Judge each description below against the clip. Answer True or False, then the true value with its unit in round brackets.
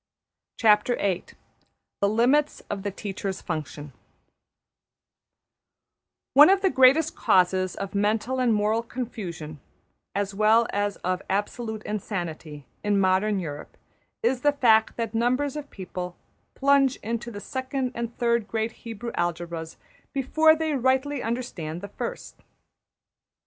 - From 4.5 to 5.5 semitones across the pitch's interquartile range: True (5.1 semitones)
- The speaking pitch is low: False (220 Hz)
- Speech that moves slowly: True (120 wpm)